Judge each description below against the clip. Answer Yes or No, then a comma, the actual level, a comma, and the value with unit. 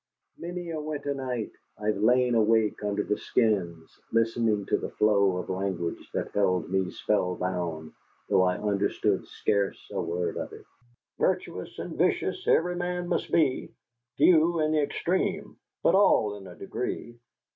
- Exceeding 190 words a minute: No, average, 155 wpm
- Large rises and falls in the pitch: Yes, wide, 7.9 semitones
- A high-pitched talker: No, low, 105 Hz